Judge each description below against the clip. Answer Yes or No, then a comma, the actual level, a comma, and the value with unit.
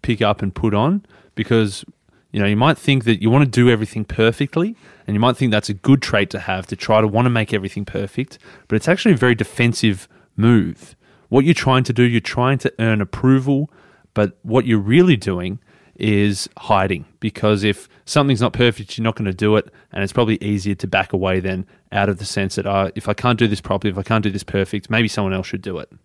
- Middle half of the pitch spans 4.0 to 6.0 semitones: No, average, 3.5 semitones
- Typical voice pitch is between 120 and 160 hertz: No, low, 110 Hz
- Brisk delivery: Yes, fast, 235 wpm